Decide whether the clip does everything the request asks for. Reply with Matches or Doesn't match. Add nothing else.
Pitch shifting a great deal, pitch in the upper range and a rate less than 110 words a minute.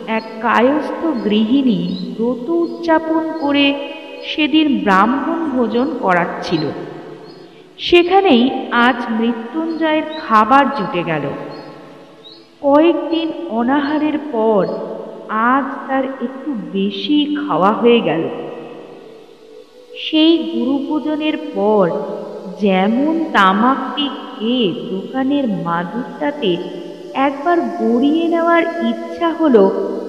Matches